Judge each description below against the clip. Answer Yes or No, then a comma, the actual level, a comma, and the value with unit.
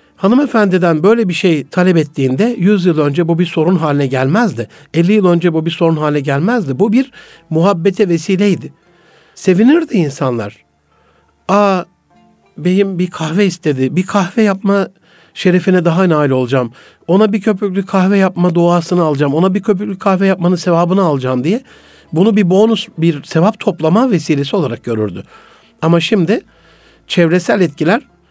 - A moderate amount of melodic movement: Yes, average, 3.9 semitones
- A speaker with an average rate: No, fast, 145 wpm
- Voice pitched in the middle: Yes, medium, 180 Hz